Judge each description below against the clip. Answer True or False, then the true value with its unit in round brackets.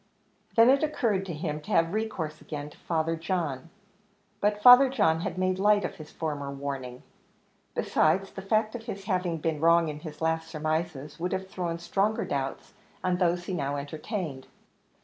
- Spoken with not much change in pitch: False (4.2 semitones)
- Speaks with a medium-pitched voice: True (170 Hz)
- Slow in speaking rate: False (175 wpm)